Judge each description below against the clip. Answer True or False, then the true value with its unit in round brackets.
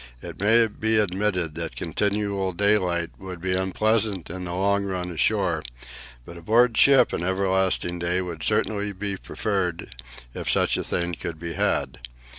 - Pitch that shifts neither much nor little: True (3.0 semitones)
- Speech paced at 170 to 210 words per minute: False (155 wpm)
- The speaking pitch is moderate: False (95 Hz)